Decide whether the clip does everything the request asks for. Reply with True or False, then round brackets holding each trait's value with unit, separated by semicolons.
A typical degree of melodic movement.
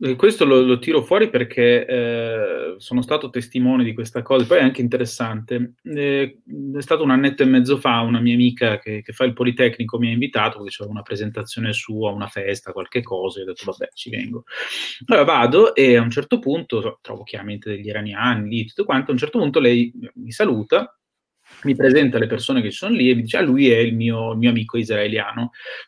True (3.0 semitones)